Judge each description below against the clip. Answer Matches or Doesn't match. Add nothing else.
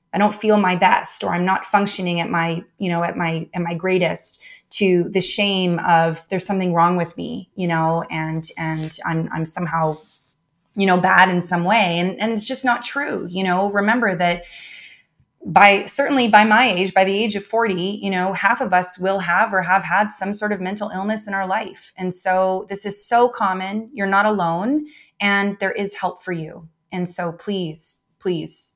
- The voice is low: Doesn't match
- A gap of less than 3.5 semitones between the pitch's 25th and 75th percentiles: Matches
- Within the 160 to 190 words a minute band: Doesn't match